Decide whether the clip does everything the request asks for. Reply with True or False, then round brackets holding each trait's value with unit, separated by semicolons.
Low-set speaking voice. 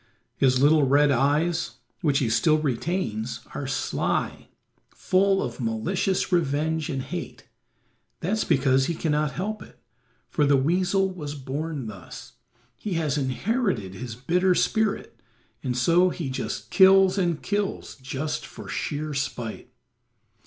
False (150 Hz)